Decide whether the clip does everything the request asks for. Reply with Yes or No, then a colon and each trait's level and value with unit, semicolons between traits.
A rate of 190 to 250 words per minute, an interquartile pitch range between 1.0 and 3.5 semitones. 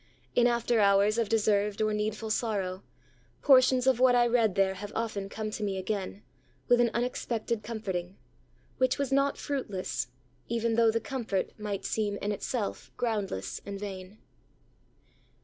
No: average, 150 wpm; average, 2.9 semitones